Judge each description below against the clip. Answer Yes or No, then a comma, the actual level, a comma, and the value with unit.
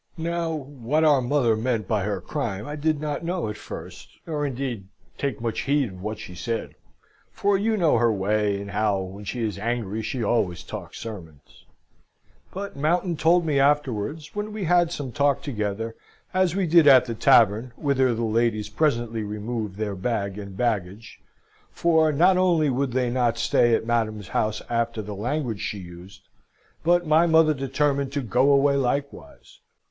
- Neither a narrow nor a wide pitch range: No, wide, 5.8 semitones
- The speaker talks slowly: No, average, 175 wpm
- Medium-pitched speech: No, low, 120 Hz